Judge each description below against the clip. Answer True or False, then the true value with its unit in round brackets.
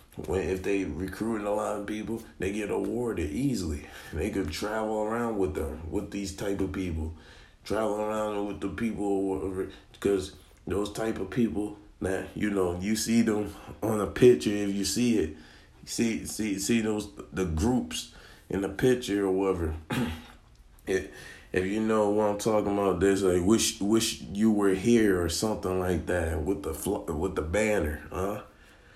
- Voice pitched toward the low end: True (100 Hz)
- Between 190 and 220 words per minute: False (175 wpm)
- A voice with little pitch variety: True (2.3 semitones)